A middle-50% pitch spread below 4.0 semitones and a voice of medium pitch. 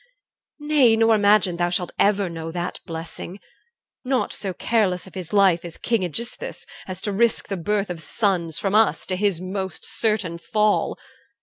No: average, 3.4 semitones; high, 195 Hz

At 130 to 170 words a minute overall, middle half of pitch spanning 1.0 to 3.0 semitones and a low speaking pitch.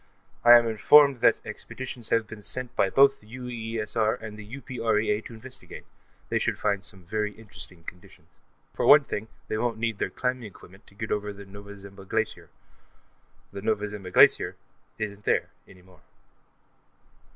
Yes: average, 165 wpm; average, 2.7 semitones; low, 110 Hz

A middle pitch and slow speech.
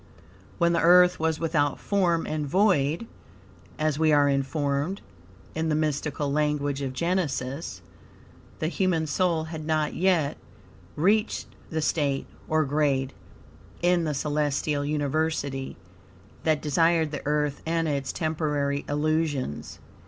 Yes: medium, 155 Hz; slow, 125 wpm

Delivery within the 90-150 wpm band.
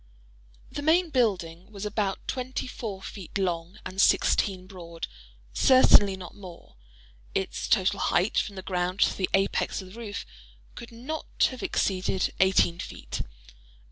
Yes: average, 140 wpm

